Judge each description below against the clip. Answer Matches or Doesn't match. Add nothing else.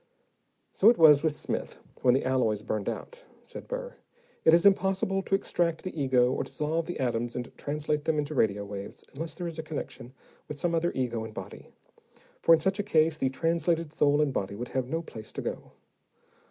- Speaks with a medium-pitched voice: Matches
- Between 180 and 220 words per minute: Matches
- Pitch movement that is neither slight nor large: Matches